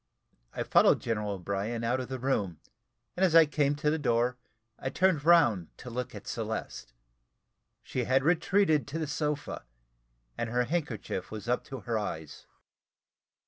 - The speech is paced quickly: No, average, 160 wpm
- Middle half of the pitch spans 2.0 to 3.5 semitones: No, average, 5.0 semitones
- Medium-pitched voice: No, low, 125 Hz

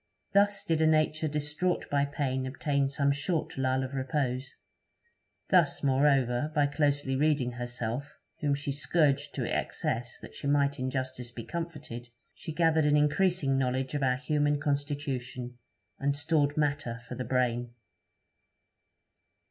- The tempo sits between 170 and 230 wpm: No, average, 140 wpm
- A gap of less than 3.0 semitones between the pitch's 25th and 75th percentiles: Yes, narrow, 2.4 semitones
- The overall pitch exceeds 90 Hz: Yes, medium, 140 Hz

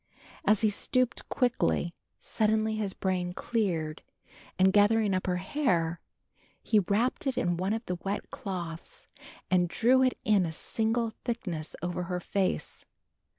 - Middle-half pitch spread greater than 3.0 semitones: Yes, average, 4.0 semitones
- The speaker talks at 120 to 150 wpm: Yes, average, 145 wpm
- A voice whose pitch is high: Yes, high, 195 Hz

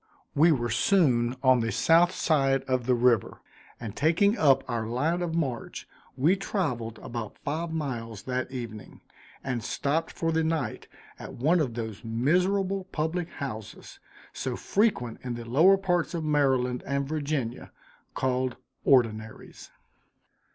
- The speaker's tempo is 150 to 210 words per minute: No, average, 140 wpm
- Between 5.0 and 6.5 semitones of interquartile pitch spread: Yes, wide, 5.4 semitones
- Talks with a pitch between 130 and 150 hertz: Yes, low, 135 Hz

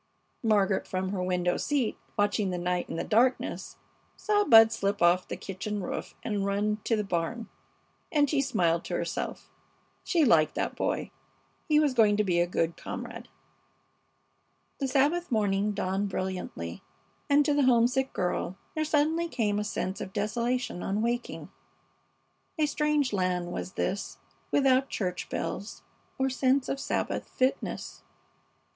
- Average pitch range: No, wide, 6.1 semitones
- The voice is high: Yes, high, 210 Hz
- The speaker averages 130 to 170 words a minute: Yes, average, 150 wpm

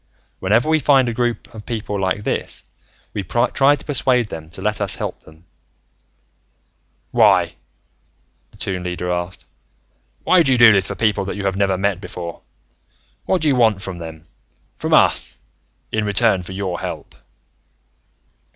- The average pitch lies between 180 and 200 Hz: No, low, 100 Hz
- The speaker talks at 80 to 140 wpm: No, average, 160 wpm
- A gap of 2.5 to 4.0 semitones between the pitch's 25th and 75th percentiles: No, average, 4.4 semitones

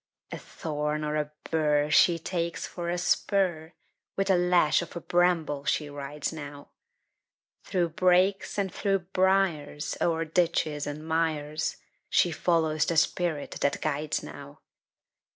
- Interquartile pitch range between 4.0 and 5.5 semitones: No, average, 2.9 semitones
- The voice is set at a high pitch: No, medium, 160 Hz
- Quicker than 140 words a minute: No, slow, 135 wpm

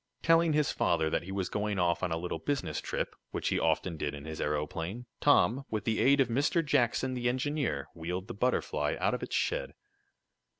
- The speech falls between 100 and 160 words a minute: No, fast, 205 wpm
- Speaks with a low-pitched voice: Yes, low, 110 Hz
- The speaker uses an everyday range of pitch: No, wide, 8.2 semitones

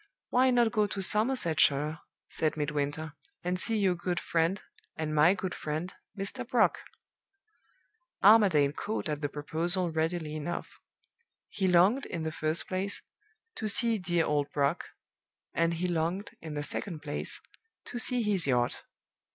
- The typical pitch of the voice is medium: Yes, medium, 170 Hz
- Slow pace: No, average, 145 wpm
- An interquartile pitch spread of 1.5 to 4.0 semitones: No, average, 4.5 semitones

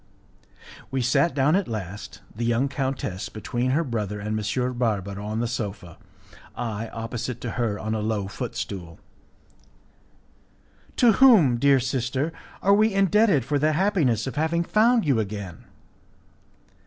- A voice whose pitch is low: Yes, low, 120 Hz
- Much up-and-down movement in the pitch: Yes, wide, 5.9 semitones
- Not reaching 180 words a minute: Yes, average, 145 wpm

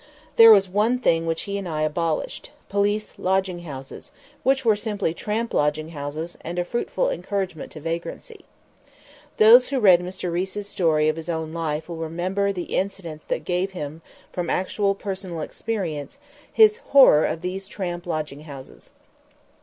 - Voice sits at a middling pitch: Yes, medium, 180 Hz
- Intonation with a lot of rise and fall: No, average, 4.0 semitones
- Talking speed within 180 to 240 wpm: No, average, 160 wpm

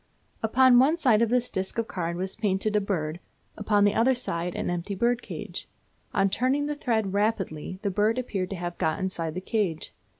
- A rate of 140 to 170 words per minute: No, average, 200 wpm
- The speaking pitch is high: Yes, high, 205 Hz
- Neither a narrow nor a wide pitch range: Yes, average, 4.4 semitones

